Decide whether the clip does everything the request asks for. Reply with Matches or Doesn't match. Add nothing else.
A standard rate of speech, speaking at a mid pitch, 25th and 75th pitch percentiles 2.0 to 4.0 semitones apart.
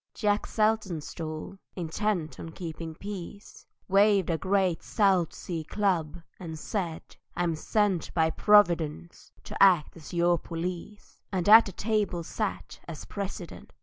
Doesn't match